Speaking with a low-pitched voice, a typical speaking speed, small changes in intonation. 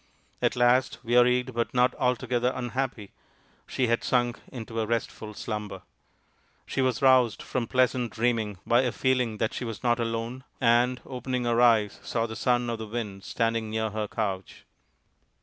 Yes: low, 120 Hz; average, 165 wpm; narrow, 2.0 semitones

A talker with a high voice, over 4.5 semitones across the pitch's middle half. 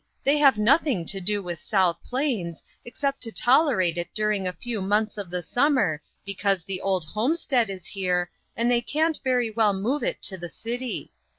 Yes: high, 210 Hz; average, 5.3 semitones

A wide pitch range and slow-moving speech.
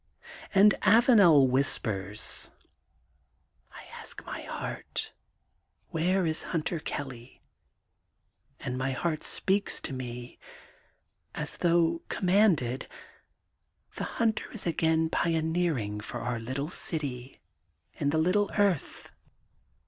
Yes: wide, 5.7 semitones; slow, 105 wpm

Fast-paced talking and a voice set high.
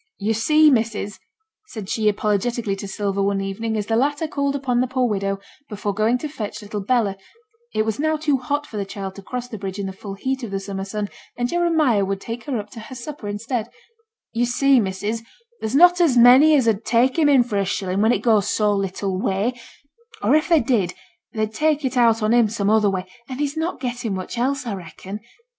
Yes: fast, 225 wpm; high, 225 Hz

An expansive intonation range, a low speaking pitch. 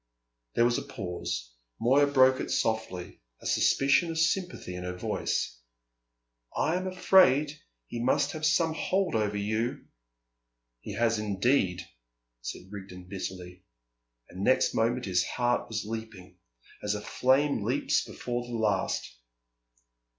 Yes: wide, 6.5 semitones; low, 115 Hz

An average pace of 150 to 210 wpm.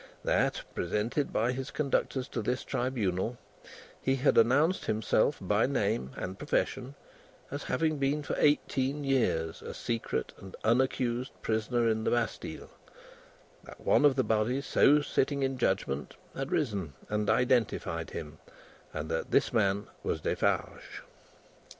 No: average, 140 wpm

